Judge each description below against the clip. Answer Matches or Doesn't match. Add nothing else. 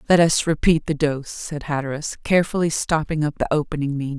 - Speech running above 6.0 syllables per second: Matches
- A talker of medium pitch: Matches